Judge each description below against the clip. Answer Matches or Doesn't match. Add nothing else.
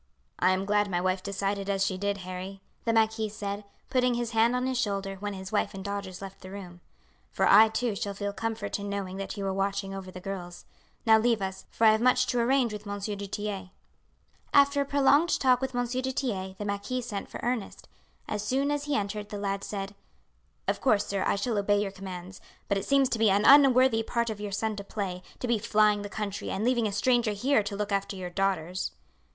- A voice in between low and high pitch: Doesn't match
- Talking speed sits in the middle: Doesn't match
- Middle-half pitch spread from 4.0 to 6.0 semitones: Doesn't match